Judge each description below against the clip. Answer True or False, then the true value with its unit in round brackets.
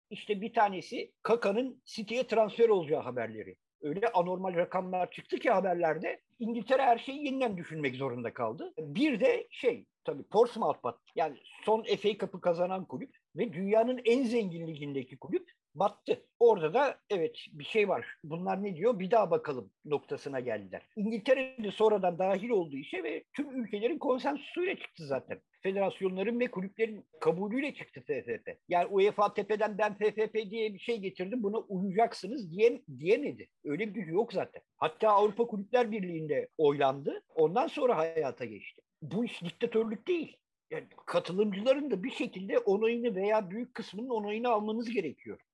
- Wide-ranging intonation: True (5.8 semitones)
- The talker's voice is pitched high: True (225 Hz)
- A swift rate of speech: True (150 wpm)